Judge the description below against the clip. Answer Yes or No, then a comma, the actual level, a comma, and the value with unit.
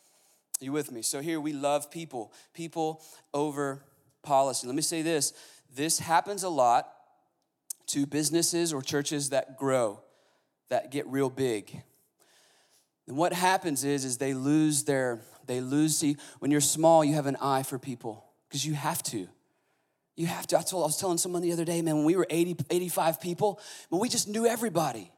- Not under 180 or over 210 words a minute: Yes, average, 185 wpm